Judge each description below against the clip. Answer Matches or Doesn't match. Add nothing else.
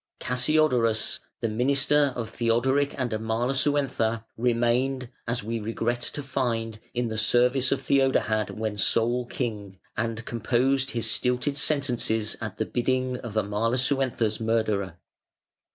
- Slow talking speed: Matches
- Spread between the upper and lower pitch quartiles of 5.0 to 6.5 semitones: Doesn't match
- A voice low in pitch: Matches